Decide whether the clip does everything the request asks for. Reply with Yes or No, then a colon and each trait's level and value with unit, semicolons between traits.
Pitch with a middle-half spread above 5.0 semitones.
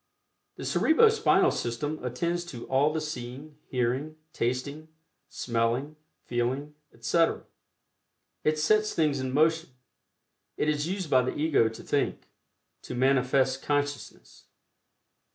No: average, 3.6 semitones